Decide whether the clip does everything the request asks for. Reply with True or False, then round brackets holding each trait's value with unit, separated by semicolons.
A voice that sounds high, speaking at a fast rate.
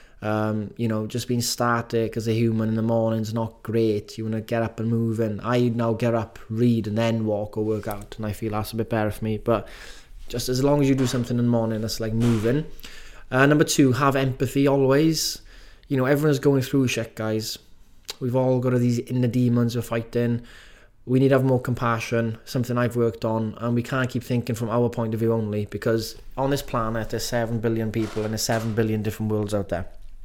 False (115 Hz; 230 wpm)